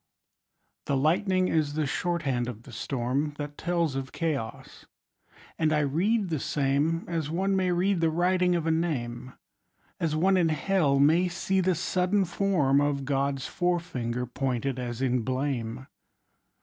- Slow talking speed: No, average, 155 wpm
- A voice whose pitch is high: No, medium, 155 Hz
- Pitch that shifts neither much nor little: Yes, average, 4.7 semitones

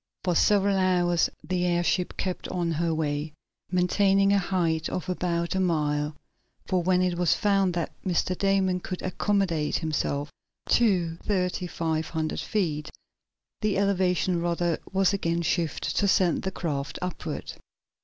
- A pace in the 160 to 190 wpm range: No, average, 145 wpm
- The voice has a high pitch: No, medium, 180 Hz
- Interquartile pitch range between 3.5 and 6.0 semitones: No, narrow, 2.4 semitones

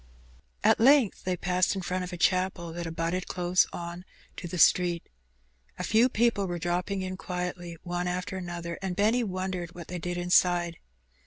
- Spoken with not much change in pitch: Yes, narrow, 1.3 semitones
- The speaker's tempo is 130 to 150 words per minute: No, average, 175 wpm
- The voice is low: No, medium, 180 Hz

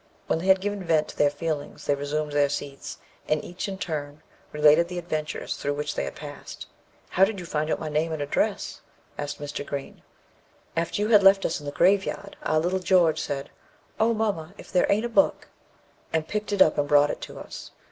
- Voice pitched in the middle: Yes, medium, 160 Hz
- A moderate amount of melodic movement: Yes, average, 4.5 semitones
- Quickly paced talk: Yes, fast, 220 wpm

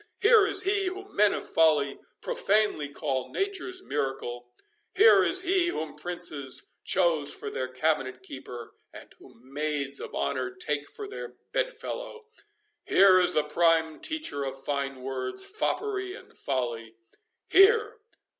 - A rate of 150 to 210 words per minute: No, slow, 135 wpm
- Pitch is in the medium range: Yes, medium, 165 Hz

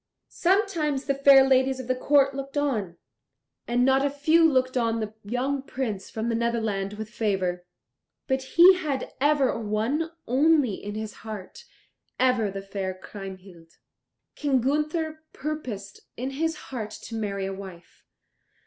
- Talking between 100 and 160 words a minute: Yes, average, 150 wpm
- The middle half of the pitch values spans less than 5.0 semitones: No, average, 5.3 semitones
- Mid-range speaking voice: No, very high, 255 Hz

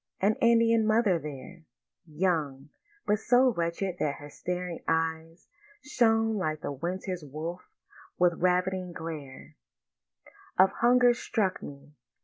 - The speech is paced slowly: Yes, slow, 120 wpm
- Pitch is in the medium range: Yes, medium, 180 Hz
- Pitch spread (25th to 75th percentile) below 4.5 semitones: No, average, 5.3 semitones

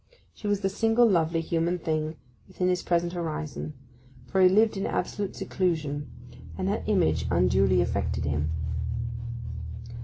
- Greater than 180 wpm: No, slow, 135 wpm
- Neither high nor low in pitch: Yes, medium, 170 Hz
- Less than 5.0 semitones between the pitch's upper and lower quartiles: Yes, average, 4.6 semitones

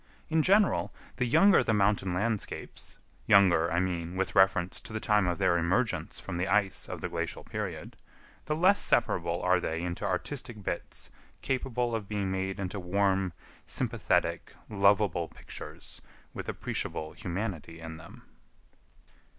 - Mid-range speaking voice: No, very low, 95 Hz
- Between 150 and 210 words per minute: No, average, 140 wpm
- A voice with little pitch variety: No, average, 3.7 semitones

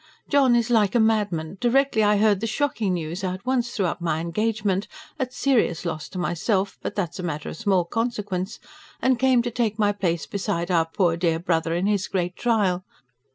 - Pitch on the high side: Yes, high, 200 Hz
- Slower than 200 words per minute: No, fast, 205 wpm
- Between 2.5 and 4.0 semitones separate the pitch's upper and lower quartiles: No, average, 4.6 semitones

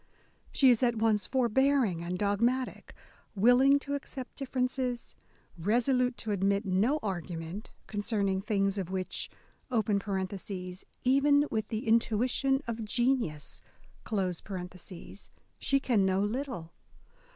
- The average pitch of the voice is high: Yes, high, 220 Hz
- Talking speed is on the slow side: Yes, slow, 105 wpm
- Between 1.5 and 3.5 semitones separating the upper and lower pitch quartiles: No, average, 4.6 semitones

